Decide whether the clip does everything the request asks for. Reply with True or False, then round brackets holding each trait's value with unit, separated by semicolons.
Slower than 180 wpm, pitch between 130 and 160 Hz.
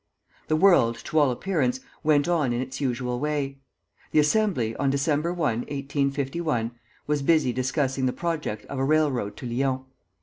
True (160 wpm; 140 Hz)